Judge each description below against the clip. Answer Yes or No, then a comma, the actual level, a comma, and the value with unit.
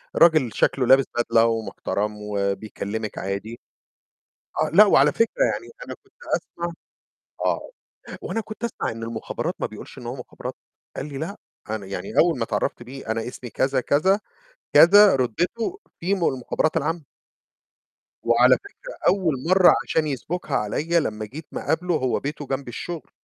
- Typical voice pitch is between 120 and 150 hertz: Yes, medium, 140 Hz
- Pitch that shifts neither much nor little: No, wide, 7.3 semitones